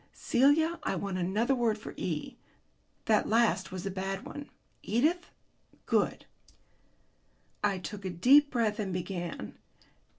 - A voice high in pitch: Yes, high, 210 Hz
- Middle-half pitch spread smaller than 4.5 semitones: No, average, 5.0 semitones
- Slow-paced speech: Yes, slow, 130 wpm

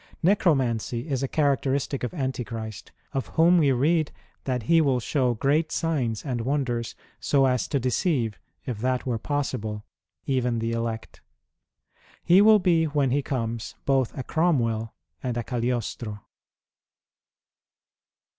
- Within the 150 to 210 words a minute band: No, slow, 135 wpm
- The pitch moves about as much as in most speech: Yes, average, 3.8 semitones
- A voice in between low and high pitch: No, low, 130 Hz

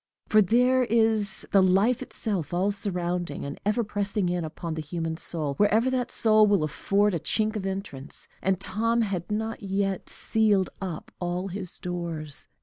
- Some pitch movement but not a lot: Yes, average, 3.6 semitones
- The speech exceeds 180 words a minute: No, average, 165 wpm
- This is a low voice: No, high, 195 Hz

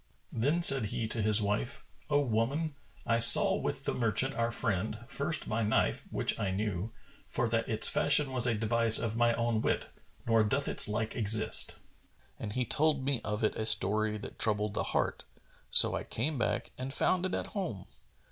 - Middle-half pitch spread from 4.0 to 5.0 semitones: No, average, 3.3 semitones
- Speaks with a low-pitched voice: Yes, low, 115 Hz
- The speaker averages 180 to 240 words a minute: Yes, average, 190 wpm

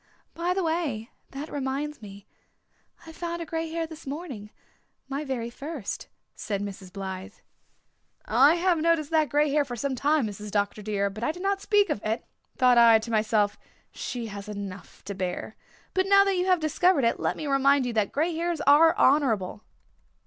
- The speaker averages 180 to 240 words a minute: Yes, average, 185 wpm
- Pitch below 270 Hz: No, very high, 275 Hz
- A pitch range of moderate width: No, wide, 7.2 semitones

